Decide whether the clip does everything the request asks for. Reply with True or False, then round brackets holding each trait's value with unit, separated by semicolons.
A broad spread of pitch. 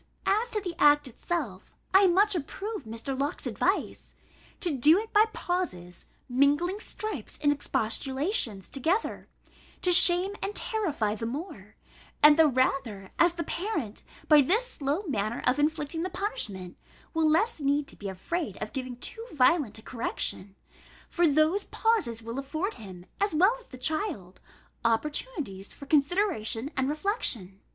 True (8.0 semitones)